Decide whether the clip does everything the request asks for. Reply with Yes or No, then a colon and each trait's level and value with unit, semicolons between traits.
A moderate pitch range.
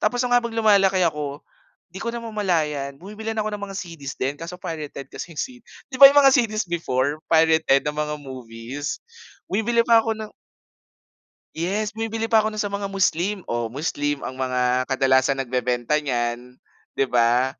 No: wide, 8.1 semitones